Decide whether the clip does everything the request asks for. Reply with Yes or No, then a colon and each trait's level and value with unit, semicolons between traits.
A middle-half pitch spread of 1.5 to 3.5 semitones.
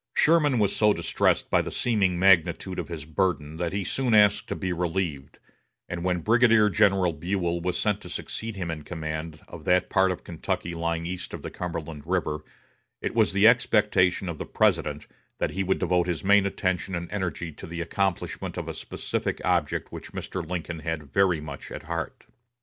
Yes: average, 2.8 semitones